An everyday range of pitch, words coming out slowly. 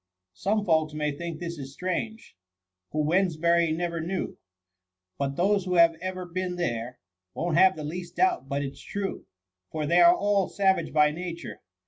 No: average, 3.2 semitones; average, 170 wpm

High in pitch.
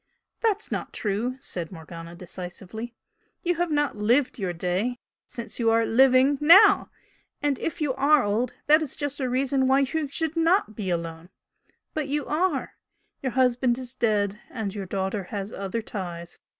Yes: high, 245 Hz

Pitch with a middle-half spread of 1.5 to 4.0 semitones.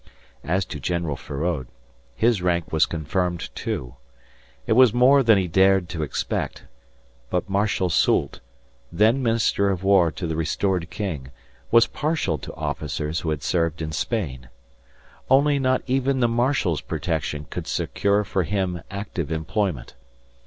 No: wide, 5.4 semitones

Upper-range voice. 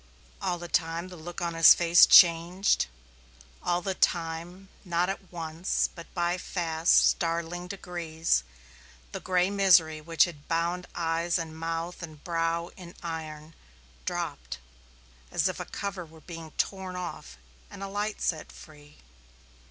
No: medium, 170 Hz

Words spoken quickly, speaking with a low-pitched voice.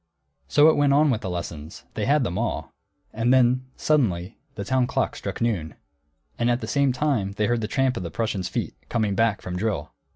Yes: fast, 215 wpm; low, 115 Hz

